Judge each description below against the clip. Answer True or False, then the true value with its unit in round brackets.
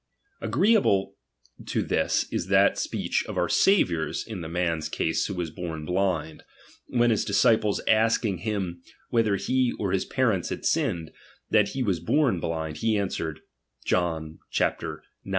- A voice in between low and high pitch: False (95 Hz)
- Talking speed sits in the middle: True (150 wpm)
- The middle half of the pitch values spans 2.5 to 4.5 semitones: False (5.2 semitones)